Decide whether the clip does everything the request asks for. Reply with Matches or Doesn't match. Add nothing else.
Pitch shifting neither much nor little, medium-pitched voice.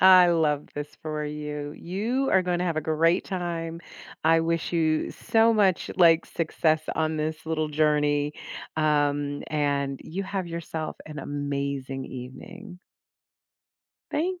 Matches